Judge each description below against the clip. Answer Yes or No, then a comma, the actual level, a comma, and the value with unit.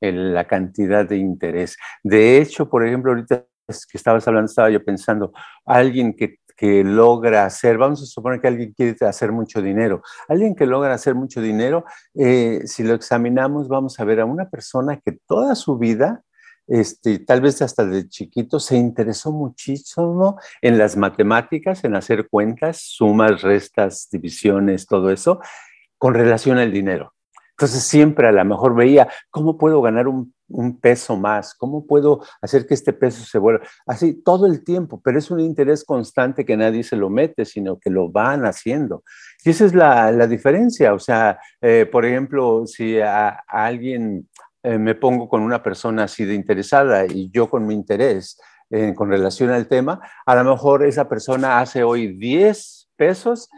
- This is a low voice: Yes, low, 120 Hz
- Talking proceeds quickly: No, average, 175 wpm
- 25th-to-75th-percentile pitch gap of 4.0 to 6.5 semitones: Yes, average, 4.7 semitones